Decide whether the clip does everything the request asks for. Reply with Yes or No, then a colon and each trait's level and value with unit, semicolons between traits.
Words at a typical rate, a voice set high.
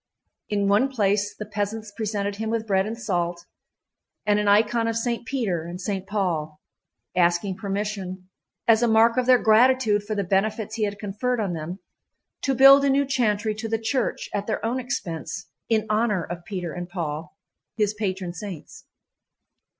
Yes: average, 175 wpm; high, 210 Hz